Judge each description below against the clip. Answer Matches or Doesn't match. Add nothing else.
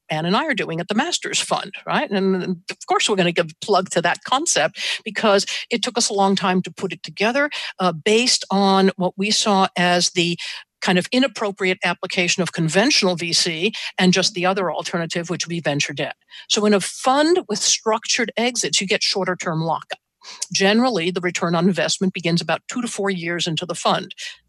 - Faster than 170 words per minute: Matches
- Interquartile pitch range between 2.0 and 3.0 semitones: Doesn't match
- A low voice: Doesn't match